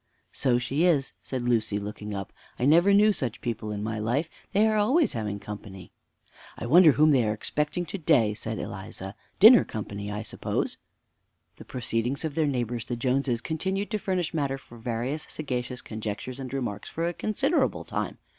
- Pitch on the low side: Yes, low, 125 Hz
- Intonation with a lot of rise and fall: Yes, wide, 6.5 semitones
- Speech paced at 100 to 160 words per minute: No, average, 180 wpm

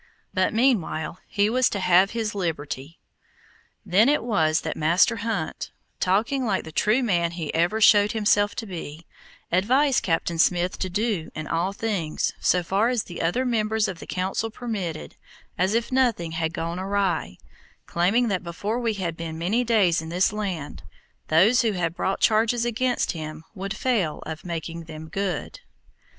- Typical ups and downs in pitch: Yes, average, 4.9 semitones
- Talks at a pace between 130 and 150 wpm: No, average, 165 wpm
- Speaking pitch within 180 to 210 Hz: Yes, high, 190 Hz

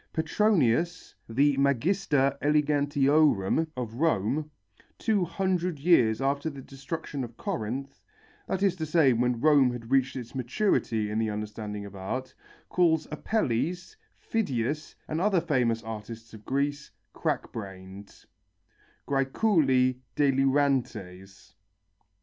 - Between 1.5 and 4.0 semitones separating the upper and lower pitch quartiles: No, wide, 5.4 semitones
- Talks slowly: Yes, slow, 115 wpm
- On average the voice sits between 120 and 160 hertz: Yes, low, 135 Hz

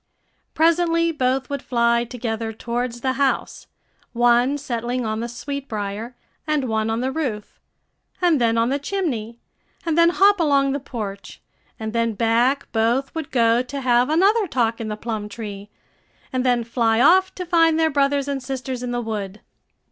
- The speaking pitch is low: No, very high, 250 Hz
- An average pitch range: Yes, average, 3.8 semitones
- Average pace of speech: Yes, average, 170 wpm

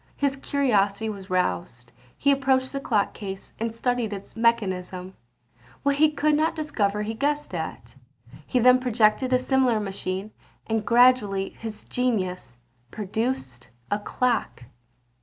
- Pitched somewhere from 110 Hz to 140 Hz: No, high, 225 Hz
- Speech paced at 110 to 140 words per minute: Yes, slow, 135 wpm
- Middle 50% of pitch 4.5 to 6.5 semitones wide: Yes, average, 4.8 semitones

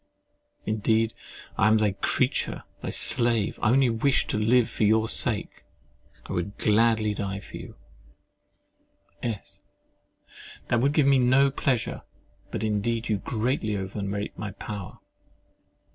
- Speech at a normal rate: No, slow, 125 wpm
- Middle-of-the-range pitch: No, low, 110 Hz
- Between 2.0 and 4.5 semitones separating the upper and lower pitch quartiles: Yes, narrow, 2.5 semitones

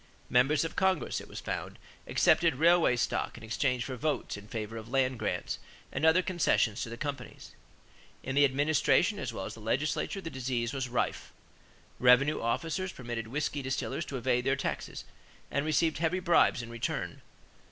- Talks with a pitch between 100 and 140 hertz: Yes, low, 135 Hz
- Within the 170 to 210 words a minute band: Yes, average, 175 wpm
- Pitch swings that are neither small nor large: Yes, average, 4.6 semitones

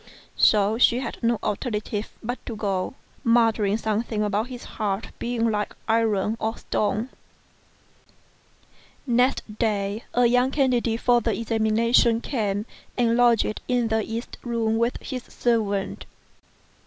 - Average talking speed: No, slow, 130 wpm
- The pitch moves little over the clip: Yes, narrow, 2.2 semitones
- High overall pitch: Yes, high, 225 Hz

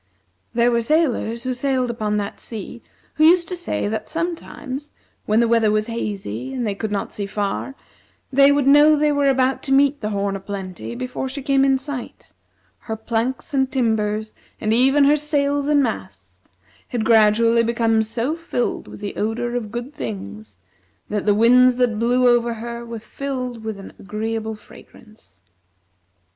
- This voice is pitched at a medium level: No, high, 235 Hz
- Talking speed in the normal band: Yes, average, 175 wpm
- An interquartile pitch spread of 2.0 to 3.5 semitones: No, average, 4.0 semitones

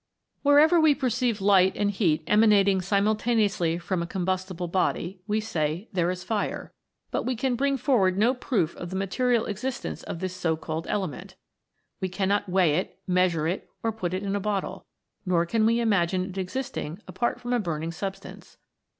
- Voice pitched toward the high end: Yes, high, 195 Hz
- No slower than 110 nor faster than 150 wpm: No, average, 175 wpm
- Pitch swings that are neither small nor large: Yes, average, 3.7 semitones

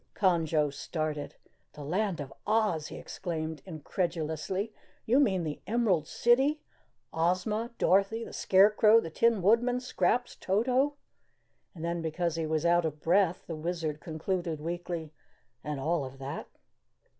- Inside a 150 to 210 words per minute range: No, average, 140 wpm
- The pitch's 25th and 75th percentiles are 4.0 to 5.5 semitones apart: Yes, average, 5.1 semitones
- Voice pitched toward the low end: No, medium, 175 Hz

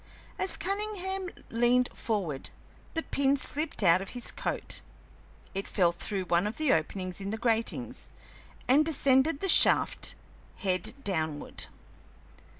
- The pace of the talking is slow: Yes, slow, 130 wpm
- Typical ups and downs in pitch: No, wide, 8.3 semitones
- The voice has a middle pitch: No, high, 230 Hz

